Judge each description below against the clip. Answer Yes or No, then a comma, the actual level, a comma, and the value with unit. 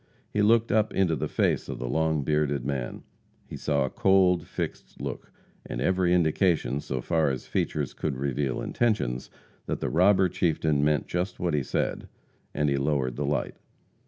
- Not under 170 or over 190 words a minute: Yes, average, 175 wpm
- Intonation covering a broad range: No, average, 4.5 semitones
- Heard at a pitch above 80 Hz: No, very low, 75 Hz